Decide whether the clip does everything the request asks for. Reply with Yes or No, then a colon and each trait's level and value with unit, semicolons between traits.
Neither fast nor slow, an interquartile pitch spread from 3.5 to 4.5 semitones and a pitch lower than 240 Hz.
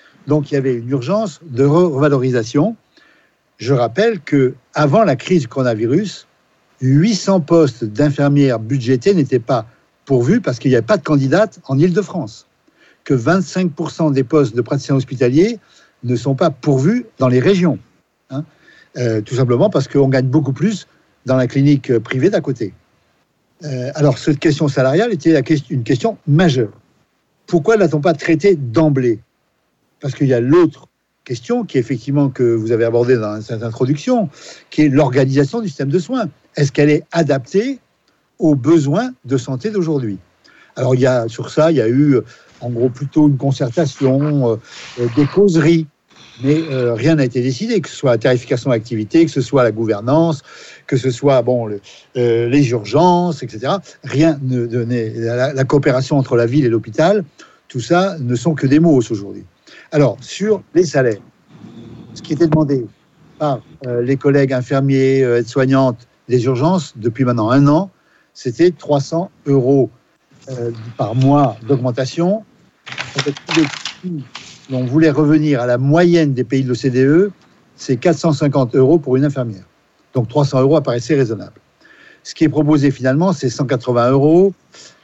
Yes: average, 165 wpm; average, 4.1 semitones; medium, 140 Hz